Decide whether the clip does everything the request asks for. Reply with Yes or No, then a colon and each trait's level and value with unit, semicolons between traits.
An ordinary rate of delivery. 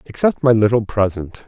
Yes: average, 165 wpm